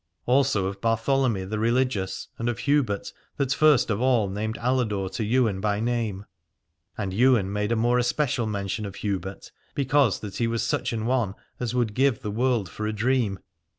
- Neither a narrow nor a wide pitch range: Yes, average, 3.6 semitones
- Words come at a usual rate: Yes, average, 185 wpm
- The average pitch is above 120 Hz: No, low, 115 Hz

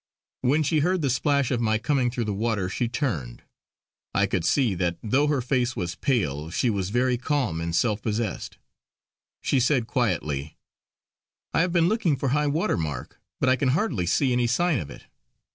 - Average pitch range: No, wide, 6.5 semitones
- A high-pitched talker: No, low, 120 Hz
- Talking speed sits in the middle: Yes, average, 190 wpm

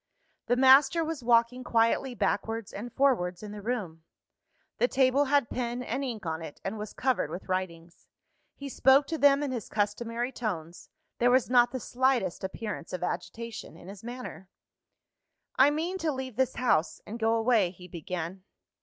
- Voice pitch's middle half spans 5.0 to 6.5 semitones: Yes, average, 5.3 semitones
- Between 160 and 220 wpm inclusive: Yes, average, 170 wpm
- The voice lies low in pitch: No, high, 235 Hz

